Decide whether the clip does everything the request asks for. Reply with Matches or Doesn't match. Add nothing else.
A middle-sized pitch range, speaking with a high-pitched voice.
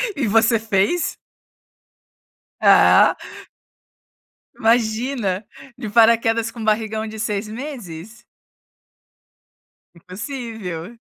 Doesn't match